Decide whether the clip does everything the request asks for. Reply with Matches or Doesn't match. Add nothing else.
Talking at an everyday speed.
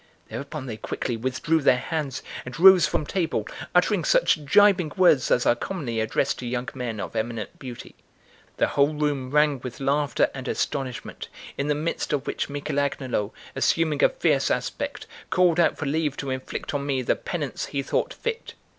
Matches